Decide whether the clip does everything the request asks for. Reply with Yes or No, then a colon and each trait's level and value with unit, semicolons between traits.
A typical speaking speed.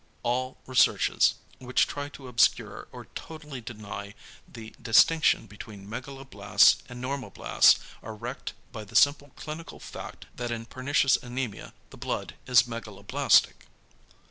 No: slow, 125 wpm